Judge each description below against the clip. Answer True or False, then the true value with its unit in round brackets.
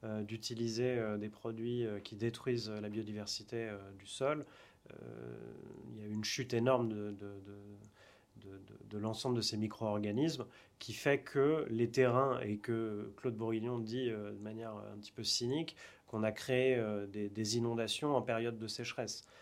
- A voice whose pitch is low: True (110 Hz)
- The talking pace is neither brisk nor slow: True (155 wpm)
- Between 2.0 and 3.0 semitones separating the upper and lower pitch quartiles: True (2.5 semitones)